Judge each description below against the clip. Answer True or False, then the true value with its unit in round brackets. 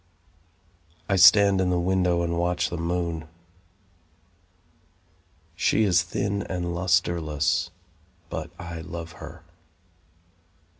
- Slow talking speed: True (100 wpm)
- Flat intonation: True (1.5 semitones)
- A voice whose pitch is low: True (85 Hz)